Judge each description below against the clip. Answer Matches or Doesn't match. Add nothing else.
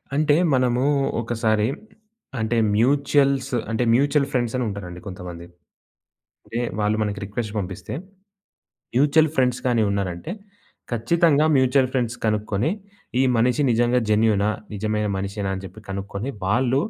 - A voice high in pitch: Doesn't match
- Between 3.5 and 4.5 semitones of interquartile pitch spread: Matches